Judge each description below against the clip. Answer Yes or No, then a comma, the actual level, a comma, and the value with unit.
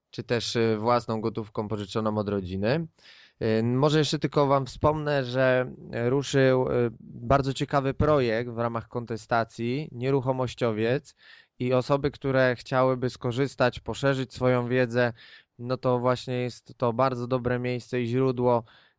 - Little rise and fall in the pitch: Yes, narrow, 2.3 semitones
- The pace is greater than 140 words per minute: No, average, 125 wpm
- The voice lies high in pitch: No, low, 125 Hz